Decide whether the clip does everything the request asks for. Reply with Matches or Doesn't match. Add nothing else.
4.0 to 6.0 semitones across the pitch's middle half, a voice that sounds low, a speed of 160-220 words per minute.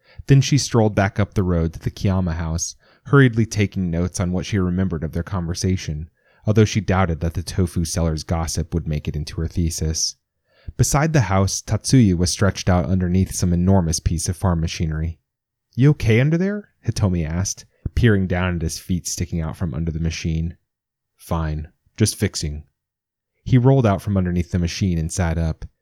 Matches